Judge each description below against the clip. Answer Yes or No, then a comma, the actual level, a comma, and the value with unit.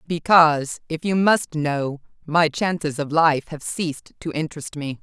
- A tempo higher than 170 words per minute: No, average, 155 wpm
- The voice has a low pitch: No, medium, 155 Hz